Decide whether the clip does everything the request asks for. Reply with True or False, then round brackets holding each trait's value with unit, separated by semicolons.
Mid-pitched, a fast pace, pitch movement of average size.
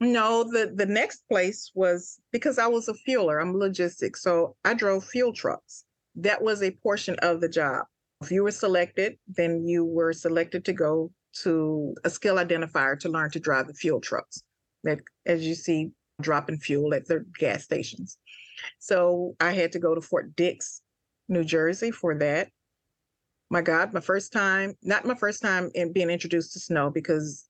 False (175 Hz; 180 wpm; 3.4 semitones)